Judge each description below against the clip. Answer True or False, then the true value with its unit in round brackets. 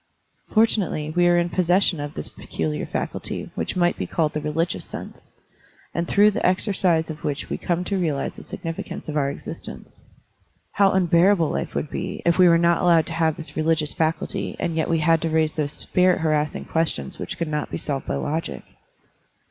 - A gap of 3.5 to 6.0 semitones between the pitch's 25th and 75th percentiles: False (2.4 semitones)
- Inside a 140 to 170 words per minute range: False (195 wpm)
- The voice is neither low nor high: True (165 Hz)